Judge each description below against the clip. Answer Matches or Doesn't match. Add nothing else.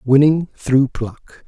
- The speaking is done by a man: Matches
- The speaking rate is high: Doesn't match